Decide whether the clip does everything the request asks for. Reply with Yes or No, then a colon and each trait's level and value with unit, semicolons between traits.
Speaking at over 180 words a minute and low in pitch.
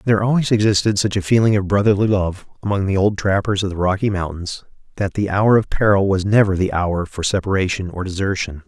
Yes: fast, 205 wpm; low, 100 Hz